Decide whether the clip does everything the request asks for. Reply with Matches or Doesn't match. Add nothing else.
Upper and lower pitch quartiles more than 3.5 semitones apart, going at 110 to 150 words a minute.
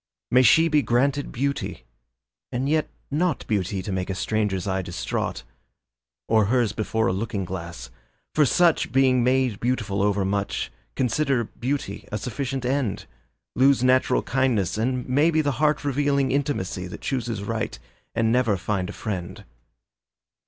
Matches